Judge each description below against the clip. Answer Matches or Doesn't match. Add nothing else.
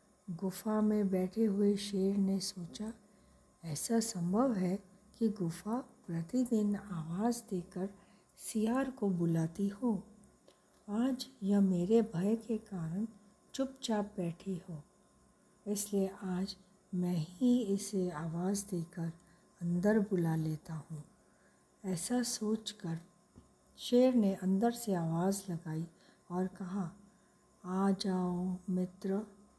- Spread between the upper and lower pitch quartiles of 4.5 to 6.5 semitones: Doesn't match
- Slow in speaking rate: Matches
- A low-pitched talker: Doesn't match